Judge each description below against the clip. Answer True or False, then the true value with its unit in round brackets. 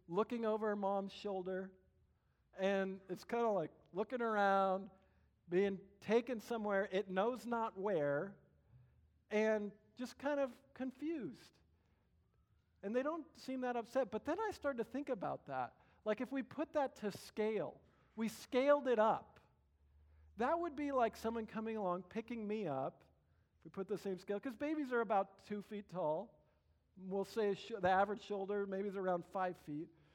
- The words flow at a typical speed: True (160 wpm)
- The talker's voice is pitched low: False (210 Hz)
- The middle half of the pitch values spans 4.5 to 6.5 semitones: False (3.9 semitones)